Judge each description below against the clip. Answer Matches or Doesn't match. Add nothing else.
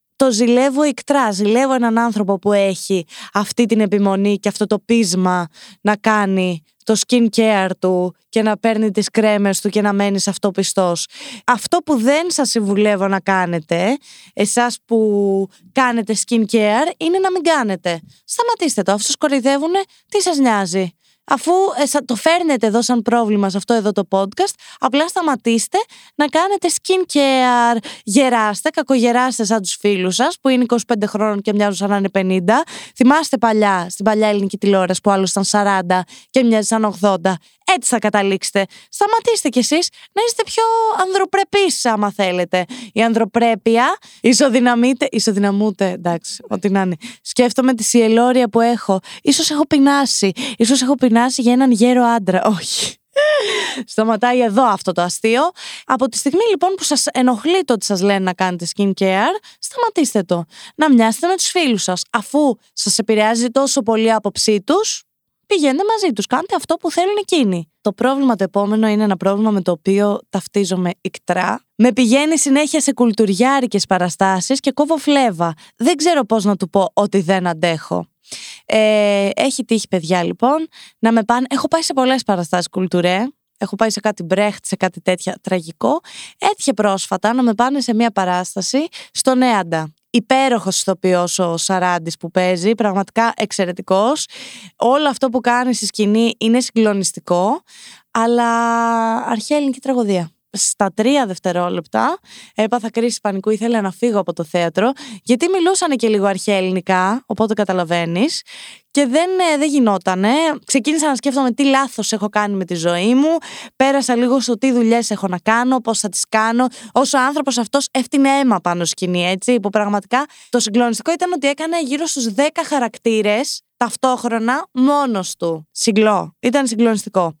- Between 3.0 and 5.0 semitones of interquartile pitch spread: Doesn't match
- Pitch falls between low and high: Doesn't match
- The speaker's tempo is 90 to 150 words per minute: Doesn't match